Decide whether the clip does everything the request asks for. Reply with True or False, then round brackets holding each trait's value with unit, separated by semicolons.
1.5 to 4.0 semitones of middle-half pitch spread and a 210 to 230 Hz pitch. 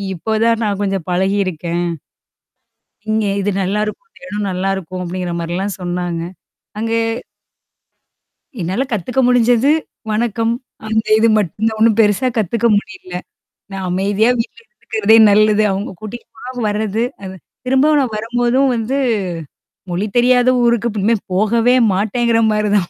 True (3.3 semitones; 215 Hz)